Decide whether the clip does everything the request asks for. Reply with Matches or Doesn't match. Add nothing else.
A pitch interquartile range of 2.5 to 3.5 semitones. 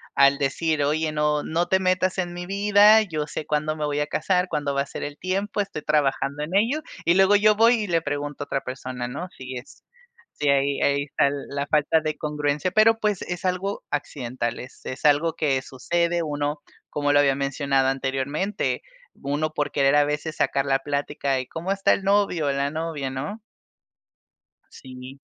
Doesn't match